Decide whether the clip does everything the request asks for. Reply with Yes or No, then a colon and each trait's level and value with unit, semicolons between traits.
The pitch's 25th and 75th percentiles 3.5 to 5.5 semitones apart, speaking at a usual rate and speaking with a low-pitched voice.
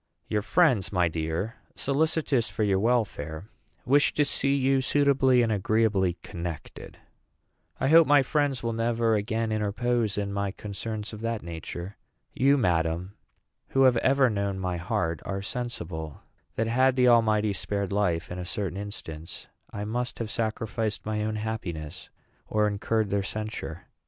Yes: average, 4.2 semitones; average, 150 wpm; low, 110 Hz